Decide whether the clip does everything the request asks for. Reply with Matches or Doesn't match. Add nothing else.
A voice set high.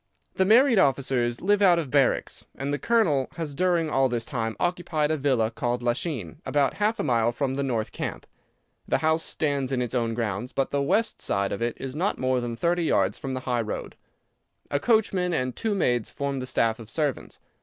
Doesn't match